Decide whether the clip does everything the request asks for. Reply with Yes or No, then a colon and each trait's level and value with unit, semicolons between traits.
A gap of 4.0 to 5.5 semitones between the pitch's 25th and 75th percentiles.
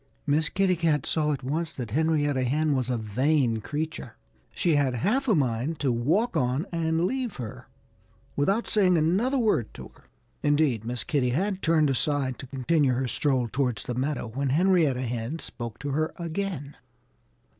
Yes: average, 4.7 semitones